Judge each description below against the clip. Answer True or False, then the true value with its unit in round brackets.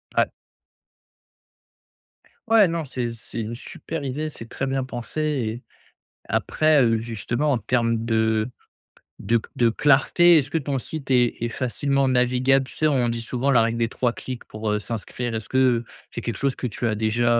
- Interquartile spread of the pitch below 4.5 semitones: True (3.0 semitones)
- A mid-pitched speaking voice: False (125 Hz)